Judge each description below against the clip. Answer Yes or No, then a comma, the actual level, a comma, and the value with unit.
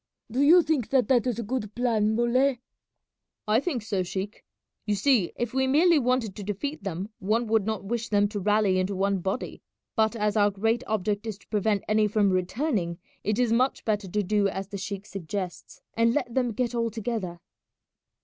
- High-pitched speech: Yes, high, 215 Hz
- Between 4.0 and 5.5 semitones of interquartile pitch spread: No, average, 3.3 semitones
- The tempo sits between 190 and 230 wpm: Yes, average, 195 wpm